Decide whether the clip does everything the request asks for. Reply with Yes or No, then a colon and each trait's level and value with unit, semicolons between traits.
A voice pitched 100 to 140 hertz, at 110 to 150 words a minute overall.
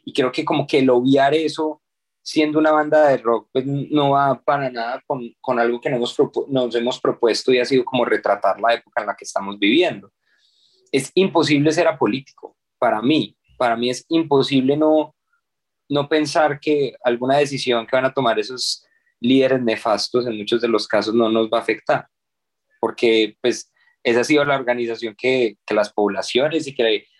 No: low, 135 Hz; fast, 190 wpm